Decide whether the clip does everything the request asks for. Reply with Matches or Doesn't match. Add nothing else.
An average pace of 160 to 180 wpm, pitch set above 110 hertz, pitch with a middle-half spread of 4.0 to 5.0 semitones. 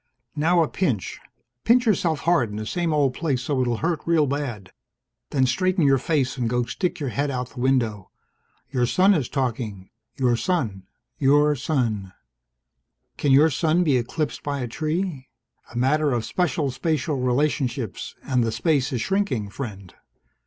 Matches